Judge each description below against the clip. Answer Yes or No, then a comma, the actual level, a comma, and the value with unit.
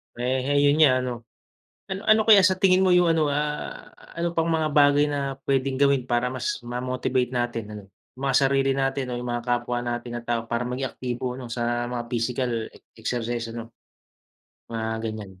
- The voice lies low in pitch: Yes, low, 130 Hz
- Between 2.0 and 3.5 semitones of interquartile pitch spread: Yes, average, 3.0 semitones